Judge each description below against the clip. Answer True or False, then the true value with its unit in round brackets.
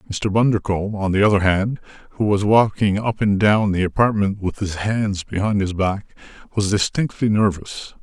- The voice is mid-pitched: False (100 Hz)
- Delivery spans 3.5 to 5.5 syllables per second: True (5.0 syllables/s)